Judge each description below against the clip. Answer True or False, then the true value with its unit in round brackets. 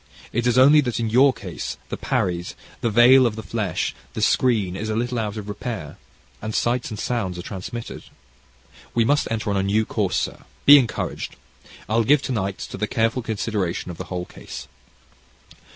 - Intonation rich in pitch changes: False (3.3 semitones)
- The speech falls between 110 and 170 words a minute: False (190 wpm)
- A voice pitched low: True (110 Hz)